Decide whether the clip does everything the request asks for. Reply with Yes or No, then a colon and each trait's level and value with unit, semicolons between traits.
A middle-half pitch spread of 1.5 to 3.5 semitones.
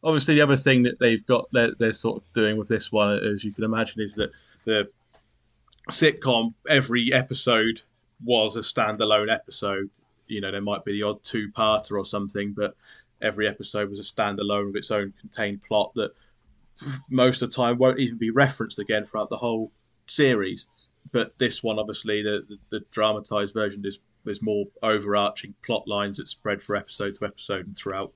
Yes: narrow, 2.6 semitones